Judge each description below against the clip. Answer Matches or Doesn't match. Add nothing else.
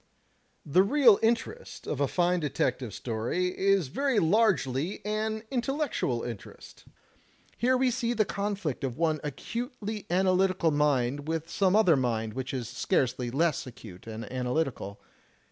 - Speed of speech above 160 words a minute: Doesn't match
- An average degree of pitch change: Doesn't match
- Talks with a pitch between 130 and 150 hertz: Doesn't match